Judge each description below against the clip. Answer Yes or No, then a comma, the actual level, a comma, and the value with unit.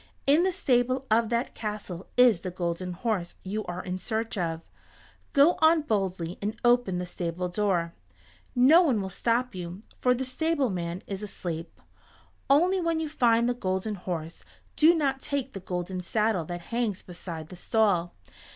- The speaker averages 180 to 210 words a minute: No, average, 165 wpm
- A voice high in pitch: Yes, high, 210 Hz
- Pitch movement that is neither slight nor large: No, wide, 5.8 semitones